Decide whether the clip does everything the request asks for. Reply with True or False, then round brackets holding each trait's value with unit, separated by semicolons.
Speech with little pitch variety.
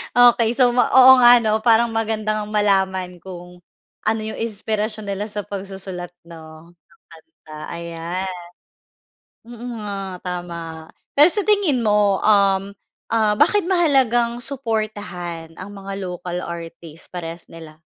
False (4.5 semitones)